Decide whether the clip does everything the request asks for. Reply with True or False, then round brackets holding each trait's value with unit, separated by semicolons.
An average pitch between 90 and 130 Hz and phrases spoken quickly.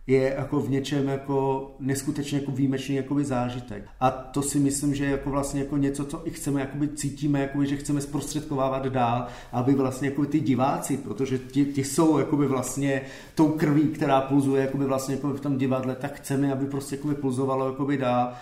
False (140 Hz; 180 wpm)